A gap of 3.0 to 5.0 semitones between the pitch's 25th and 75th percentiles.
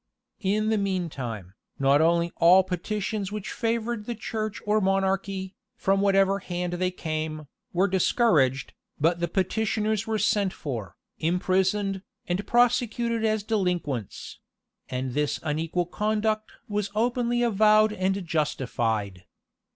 Yes: average, 4.5 semitones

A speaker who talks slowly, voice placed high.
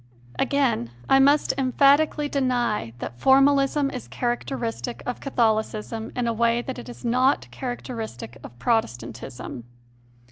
Yes: slow, 120 wpm; high, 245 Hz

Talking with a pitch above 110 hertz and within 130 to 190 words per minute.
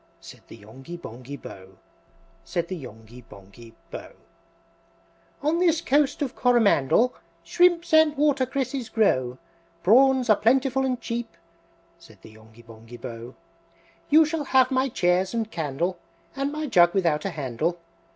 Yes: high, 190 Hz; average, 140 wpm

